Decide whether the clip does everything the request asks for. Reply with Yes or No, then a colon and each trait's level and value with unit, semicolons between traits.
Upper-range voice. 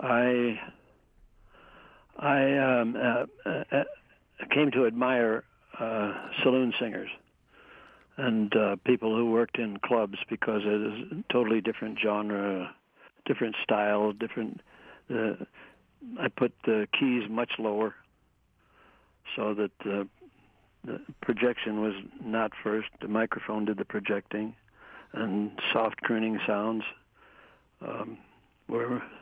No: low, 110 Hz